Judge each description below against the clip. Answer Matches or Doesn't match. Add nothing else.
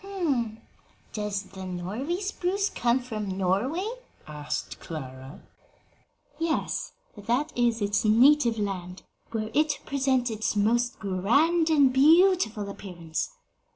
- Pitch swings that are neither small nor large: Doesn't match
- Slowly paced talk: Matches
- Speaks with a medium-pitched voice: Doesn't match